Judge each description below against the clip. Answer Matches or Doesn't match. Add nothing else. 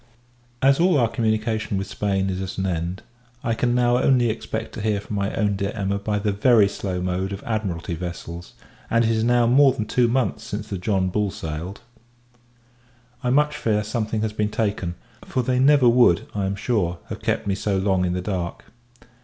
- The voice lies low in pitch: Matches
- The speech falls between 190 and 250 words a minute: Matches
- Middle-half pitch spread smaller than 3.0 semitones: Doesn't match